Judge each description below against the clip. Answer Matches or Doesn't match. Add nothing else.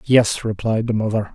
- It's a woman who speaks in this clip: Doesn't match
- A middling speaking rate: Matches